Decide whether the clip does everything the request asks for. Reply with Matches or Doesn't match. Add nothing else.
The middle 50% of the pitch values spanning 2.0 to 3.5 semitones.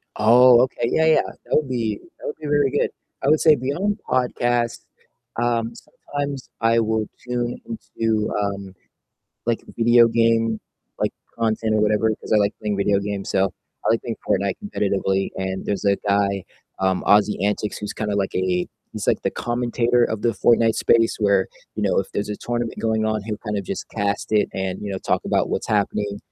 Matches